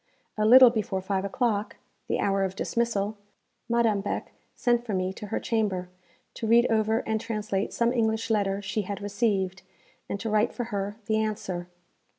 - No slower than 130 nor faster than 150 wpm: No, average, 170 wpm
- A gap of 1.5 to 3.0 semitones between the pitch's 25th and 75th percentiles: Yes, narrow, 2.5 semitones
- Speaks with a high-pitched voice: Yes, high, 215 Hz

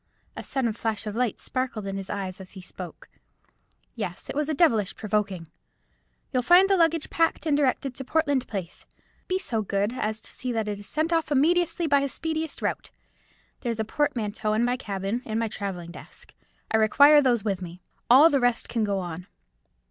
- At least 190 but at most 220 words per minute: Yes, average, 195 wpm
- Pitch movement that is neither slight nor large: No, wide, 6.1 semitones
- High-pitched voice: Yes, high, 235 Hz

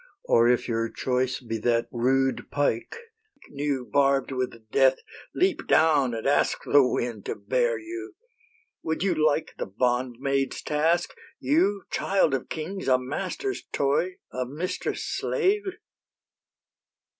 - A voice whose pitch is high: No, medium, 140 Hz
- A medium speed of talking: No, slow, 130 wpm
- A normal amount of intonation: No, wide, 5.7 semitones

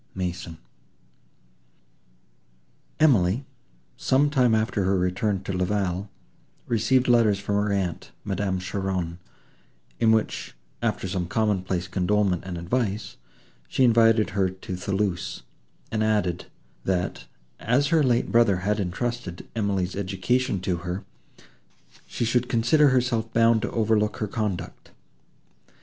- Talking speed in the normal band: No, slow, 125 wpm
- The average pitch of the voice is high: No, low, 105 Hz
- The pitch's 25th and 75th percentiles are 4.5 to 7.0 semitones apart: No, average, 3.8 semitones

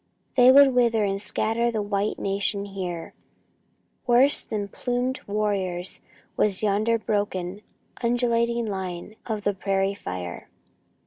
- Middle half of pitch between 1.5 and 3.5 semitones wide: Yes, average, 3.2 semitones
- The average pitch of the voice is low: No, high, 205 Hz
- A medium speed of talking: No, slow, 120 wpm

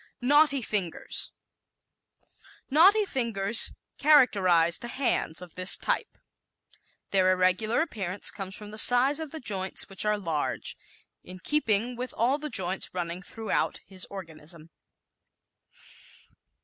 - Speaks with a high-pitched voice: Yes, high, 210 Hz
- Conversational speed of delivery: No, slow, 125 wpm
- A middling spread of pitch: No, wide, 6.0 semitones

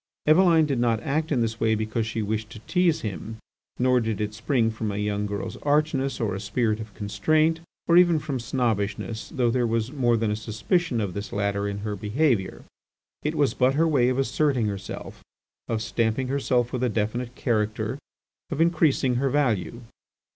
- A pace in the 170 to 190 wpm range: Yes, average, 185 wpm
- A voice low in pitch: Yes, low, 115 Hz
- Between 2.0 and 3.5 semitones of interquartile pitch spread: No, average, 4.4 semitones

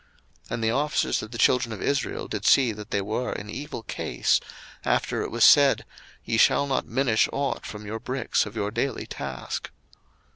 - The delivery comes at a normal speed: Yes, average, 190 wpm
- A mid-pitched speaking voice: No, low, 115 Hz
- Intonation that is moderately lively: Yes, average, 3.9 semitones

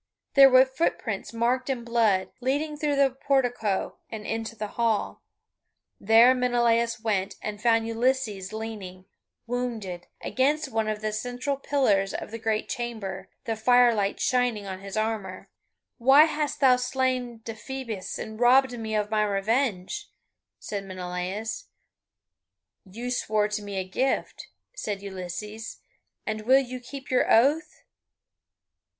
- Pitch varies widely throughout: No, average, 3.4 semitones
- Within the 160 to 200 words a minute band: No, slow, 135 wpm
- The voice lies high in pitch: Yes, high, 225 Hz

